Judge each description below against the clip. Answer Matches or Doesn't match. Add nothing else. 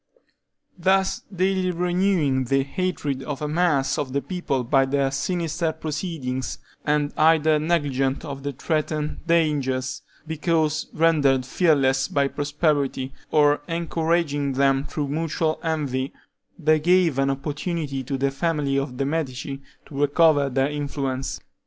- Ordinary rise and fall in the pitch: Matches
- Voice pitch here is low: Doesn't match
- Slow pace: Matches